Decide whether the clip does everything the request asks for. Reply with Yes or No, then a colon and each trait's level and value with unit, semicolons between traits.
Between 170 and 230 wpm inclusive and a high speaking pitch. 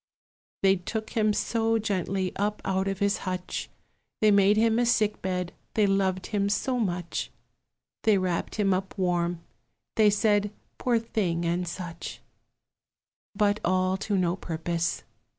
No: average, 145 wpm; high, 195 Hz